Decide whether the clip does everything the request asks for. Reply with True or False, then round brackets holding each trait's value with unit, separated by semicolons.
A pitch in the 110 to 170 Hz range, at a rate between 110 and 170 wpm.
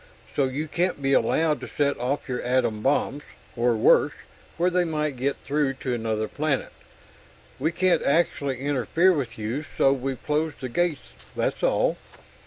True (140 Hz; 165 wpm)